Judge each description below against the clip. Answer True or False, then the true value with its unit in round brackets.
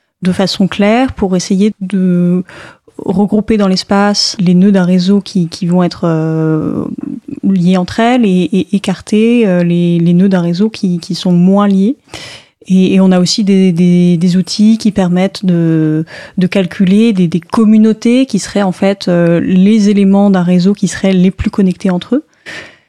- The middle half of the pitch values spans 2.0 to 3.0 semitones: True (2.6 semitones)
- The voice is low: False (190 Hz)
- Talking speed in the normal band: True (175 wpm)